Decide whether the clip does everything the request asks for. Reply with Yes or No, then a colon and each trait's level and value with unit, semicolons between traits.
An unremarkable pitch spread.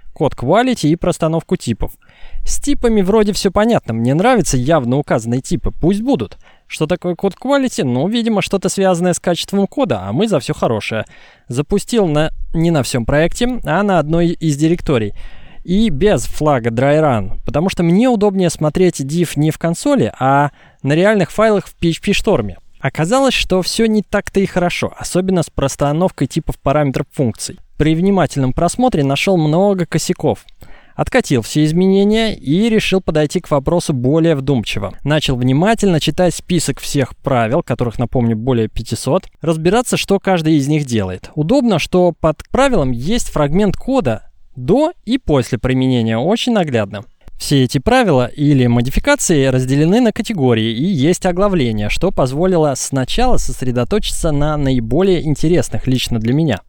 No: wide, 6.4 semitones